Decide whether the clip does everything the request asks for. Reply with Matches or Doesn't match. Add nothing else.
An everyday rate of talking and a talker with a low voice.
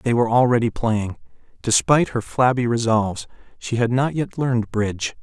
Matches